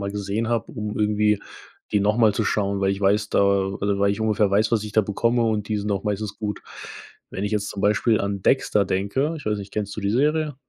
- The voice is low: Yes, low, 105 Hz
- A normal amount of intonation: No, narrow, 1.5 semitones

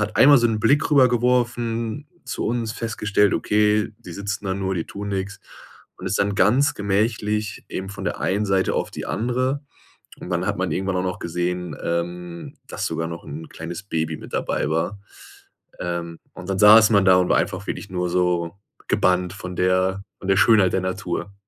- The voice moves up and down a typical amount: Yes, average, 3.2 semitones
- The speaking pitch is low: Yes, very low, 95 Hz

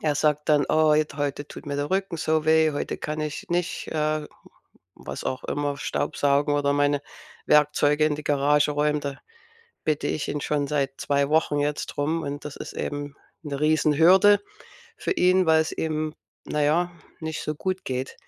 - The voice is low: No, medium, 150 Hz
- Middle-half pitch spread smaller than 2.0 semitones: Yes, narrow, 1.5 semitones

